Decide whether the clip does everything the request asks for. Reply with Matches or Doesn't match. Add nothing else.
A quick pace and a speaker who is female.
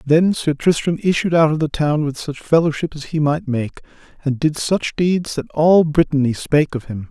Doesn't match